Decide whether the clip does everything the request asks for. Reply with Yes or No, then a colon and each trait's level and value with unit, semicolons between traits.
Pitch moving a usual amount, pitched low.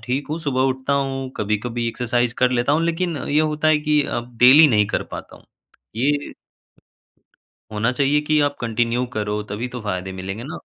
Yes: average, 4.1 semitones; low, 125 Hz